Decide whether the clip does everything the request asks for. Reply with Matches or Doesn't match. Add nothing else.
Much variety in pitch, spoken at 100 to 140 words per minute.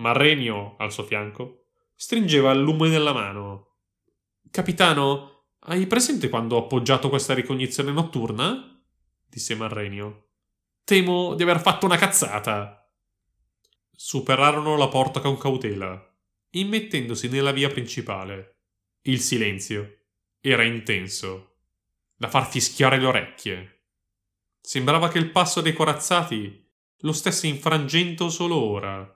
Matches